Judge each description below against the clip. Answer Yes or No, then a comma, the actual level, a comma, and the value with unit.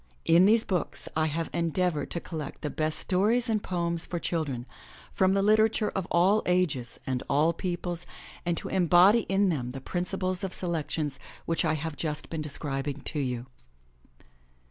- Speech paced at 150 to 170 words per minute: Yes, average, 165 wpm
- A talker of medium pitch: Yes, medium, 170 Hz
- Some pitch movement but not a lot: Yes, average, 3.6 semitones